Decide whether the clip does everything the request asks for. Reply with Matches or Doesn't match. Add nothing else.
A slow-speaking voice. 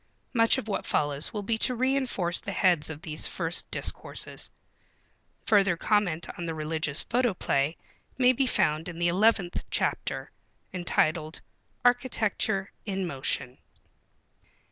Matches